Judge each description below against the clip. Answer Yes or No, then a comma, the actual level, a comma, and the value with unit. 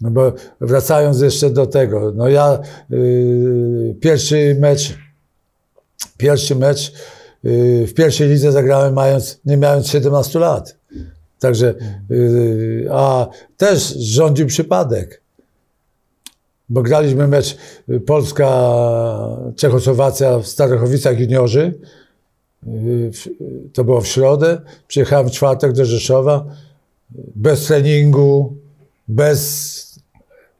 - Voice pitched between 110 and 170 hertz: Yes, low, 135 Hz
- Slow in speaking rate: Yes, slow, 100 wpm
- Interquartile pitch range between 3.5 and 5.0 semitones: No, average, 2.9 semitones